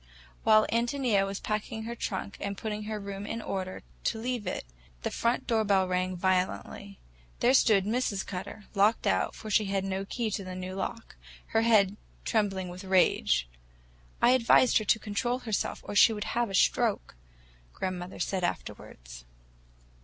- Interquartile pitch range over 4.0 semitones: No, average, 3.0 semitones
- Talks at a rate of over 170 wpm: No, average, 160 wpm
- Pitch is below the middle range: No, high, 205 Hz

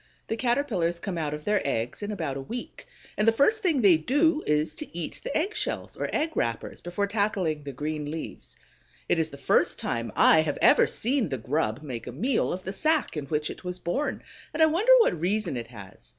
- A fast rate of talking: Yes, fast, 220 wpm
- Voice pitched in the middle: Yes, medium, 175 Hz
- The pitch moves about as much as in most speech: No, wide, 8.7 semitones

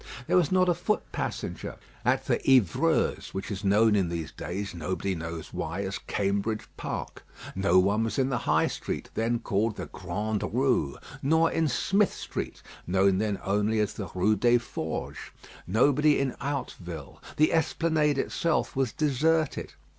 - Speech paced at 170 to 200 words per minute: No, average, 160 wpm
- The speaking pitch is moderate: No, low, 110 Hz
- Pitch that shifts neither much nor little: No, wide, 6.5 semitones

